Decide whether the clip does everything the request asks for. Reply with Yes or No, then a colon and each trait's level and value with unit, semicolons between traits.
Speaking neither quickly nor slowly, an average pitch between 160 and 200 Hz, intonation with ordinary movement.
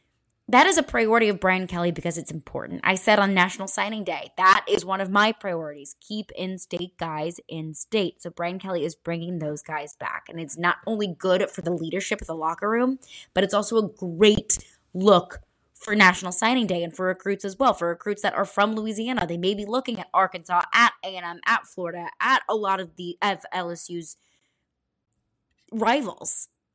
Yes: average, 195 wpm; medium, 185 Hz; average, 3.3 semitones